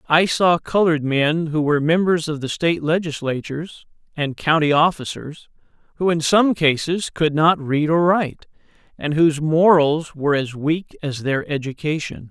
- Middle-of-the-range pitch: Yes, medium, 155 Hz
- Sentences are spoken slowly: No, average, 155 wpm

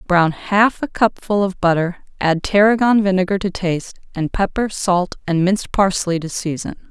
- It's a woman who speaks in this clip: Yes, female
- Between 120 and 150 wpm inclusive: No, average, 165 wpm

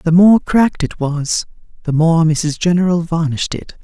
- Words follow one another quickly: No, average, 170 wpm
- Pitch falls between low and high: Yes, medium, 165 Hz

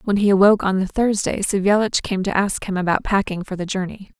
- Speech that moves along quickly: Yes, fast, 230 wpm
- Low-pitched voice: No, high, 195 Hz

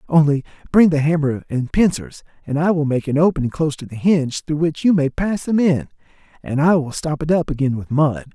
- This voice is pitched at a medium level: Yes, medium, 150 Hz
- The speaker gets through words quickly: Yes, fast, 230 wpm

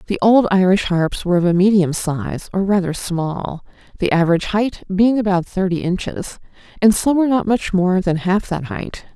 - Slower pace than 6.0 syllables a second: Yes, 5.0 syllables/s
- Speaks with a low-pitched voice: No, high, 190 Hz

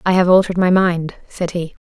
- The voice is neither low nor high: Yes, medium, 180 Hz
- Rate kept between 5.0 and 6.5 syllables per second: Yes, 5.6 syllables/s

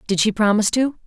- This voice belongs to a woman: Yes, female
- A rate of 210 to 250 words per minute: Yes, fast, 225 wpm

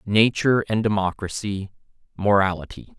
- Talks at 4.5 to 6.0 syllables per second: Yes, 4.9 syllables/s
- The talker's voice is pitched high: No, low, 105 Hz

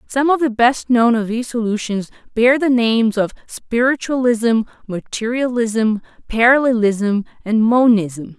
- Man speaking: No, female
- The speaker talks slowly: Yes, slow, 120 wpm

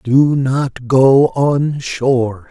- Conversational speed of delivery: No, slow, 120 wpm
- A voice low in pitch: Yes, low, 130 Hz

